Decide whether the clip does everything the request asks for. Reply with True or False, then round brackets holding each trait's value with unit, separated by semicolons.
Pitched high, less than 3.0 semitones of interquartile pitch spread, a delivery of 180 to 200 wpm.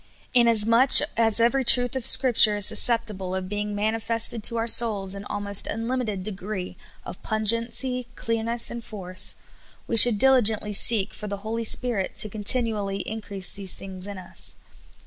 False (220 Hz; 2.6 semitones; 165 wpm)